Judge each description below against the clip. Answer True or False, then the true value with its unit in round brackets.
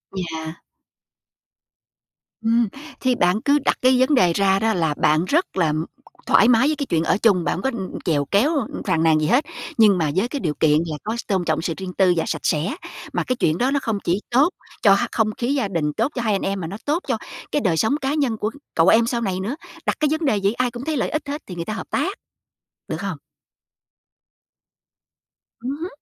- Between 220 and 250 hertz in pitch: False (210 Hz)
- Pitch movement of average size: False (6.9 semitones)